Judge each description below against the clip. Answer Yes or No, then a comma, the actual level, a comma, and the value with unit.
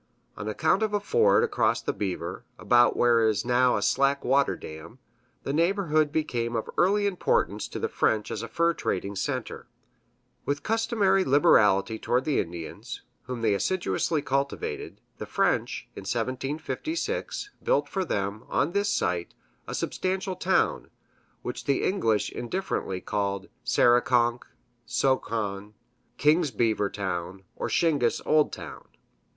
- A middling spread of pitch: No, wide, 8.9 semitones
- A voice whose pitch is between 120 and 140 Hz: Yes, low, 130 Hz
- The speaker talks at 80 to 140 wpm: Yes, slow, 135 wpm